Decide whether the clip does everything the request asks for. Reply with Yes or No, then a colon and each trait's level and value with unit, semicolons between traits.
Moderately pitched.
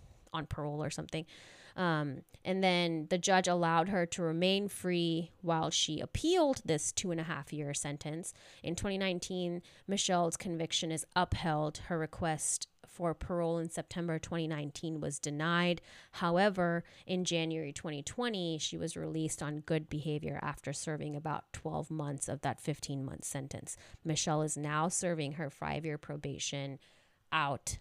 Yes: medium, 160 Hz